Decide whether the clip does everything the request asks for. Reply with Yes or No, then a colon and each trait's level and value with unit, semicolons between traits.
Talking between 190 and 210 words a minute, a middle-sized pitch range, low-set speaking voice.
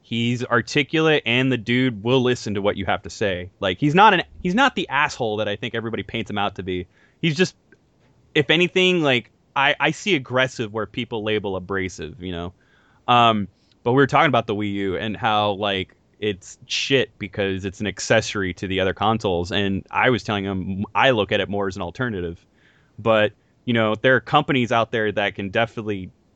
Yes: fast, 205 wpm; average, 4.1 semitones; low, 110 Hz